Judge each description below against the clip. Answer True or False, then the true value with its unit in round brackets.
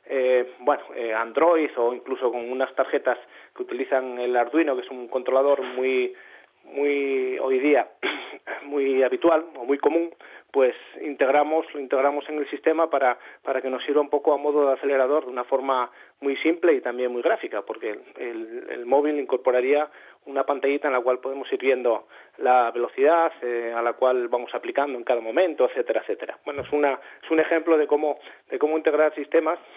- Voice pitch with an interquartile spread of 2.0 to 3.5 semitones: False (3.9 semitones)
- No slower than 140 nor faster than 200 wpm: True (185 wpm)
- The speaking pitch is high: False (140 Hz)